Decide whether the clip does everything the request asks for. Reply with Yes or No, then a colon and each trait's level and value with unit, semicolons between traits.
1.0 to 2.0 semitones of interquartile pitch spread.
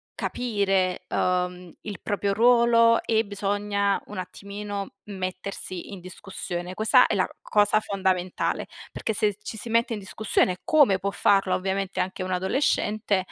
No: narrow, 2.4 semitones